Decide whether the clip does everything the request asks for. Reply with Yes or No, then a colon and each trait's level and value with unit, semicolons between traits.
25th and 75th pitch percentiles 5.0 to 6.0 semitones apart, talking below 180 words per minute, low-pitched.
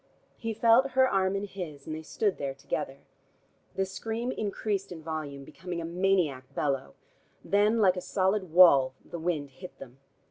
No: average, 5.3 semitones; average, 170 wpm; medium, 180 Hz